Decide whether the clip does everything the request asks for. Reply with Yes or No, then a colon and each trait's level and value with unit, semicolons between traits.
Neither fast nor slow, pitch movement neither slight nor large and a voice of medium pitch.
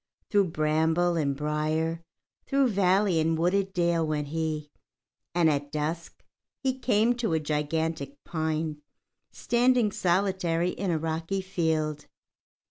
No: slow, 125 wpm; average, 3.7 semitones; medium, 165 Hz